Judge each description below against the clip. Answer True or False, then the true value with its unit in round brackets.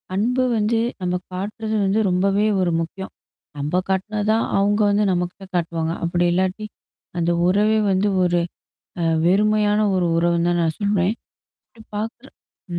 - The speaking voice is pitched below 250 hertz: True (190 Hz)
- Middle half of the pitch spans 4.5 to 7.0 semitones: False (3.3 semitones)